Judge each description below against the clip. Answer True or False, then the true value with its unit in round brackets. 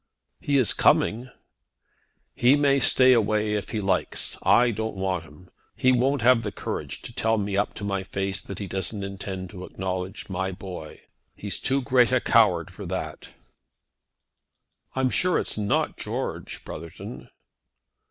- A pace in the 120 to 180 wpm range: True (160 wpm)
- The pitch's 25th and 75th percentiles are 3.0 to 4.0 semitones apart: False (4.4 semitones)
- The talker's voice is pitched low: True (105 Hz)